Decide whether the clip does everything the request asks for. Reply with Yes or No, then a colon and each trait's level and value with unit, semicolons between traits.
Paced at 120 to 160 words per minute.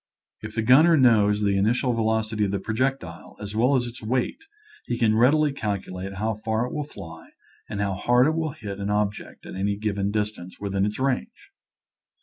No: average, 195 wpm